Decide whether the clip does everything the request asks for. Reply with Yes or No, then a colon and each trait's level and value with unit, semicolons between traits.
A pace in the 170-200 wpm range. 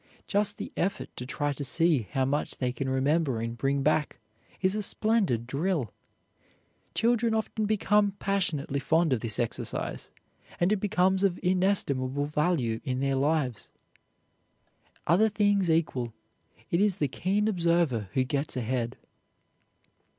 No: average, 140 wpm